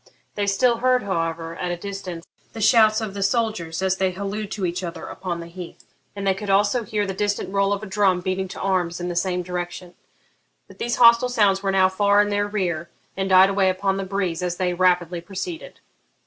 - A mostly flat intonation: Yes, narrow, 2.3 semitones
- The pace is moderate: No, fast, 220 wpm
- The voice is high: Yes, high, 195 Hz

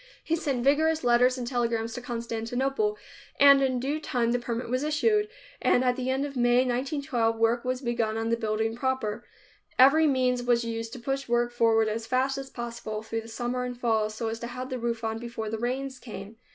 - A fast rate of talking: Yes, fast, 210 wpm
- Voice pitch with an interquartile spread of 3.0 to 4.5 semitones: No, narrow, 2.5 semitones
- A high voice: Yes, high, 245 Hz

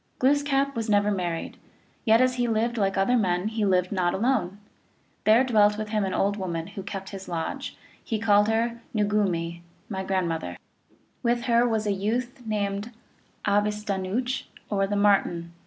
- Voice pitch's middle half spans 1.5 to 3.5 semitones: Yes, average, 3.2 semitones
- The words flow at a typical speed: Yes, average, 170 wpm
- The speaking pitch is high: Yes, high, 205 Hz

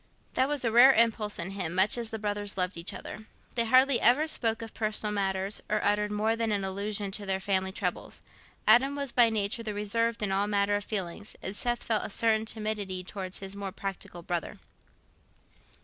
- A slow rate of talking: No, average, 195 wpm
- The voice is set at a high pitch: Yes, high, 210 Hz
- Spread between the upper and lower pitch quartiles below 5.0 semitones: Yes, average, 2.7 semitones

